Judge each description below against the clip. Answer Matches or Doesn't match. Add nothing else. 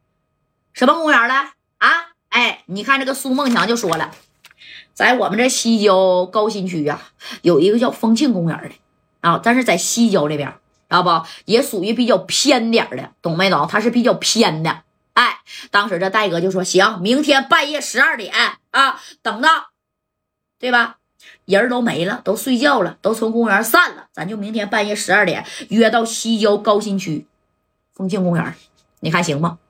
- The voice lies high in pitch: Matches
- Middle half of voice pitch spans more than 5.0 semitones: Matches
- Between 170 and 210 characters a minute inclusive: Doesn't match